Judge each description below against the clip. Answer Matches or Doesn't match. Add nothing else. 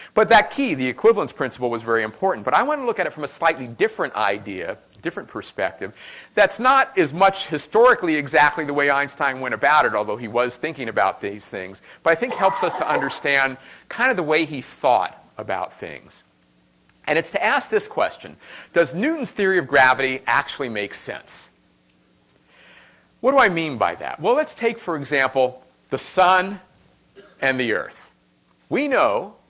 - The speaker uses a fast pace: Doesn't match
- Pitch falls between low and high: Matches